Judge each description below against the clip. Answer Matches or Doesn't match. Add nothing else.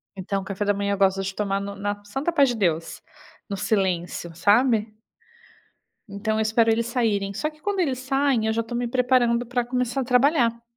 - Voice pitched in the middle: Doesn't match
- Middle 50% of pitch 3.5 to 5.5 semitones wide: Matches